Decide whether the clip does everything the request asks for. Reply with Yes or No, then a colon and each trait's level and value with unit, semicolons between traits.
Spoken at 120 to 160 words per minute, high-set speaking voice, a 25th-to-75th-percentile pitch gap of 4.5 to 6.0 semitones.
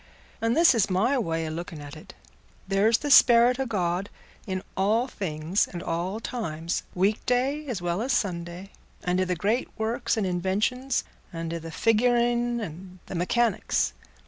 Yes: average, 155 wpm; high, 195 Hz; wide, 5.5 semitones